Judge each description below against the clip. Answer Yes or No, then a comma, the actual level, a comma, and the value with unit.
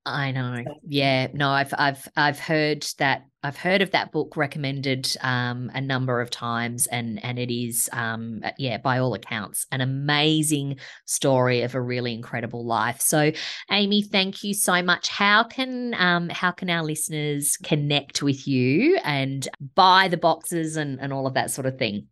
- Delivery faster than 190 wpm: No, average, 175 wpm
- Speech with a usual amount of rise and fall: Yes, average, 4.4 semitones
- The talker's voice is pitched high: No, medium, 140 Hz